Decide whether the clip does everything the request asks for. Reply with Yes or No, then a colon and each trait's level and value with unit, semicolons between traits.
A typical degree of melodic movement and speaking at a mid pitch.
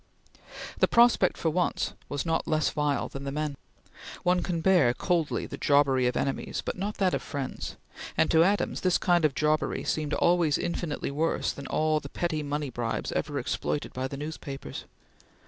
Yes: average, 3.5 semitones; medium, 155 Hz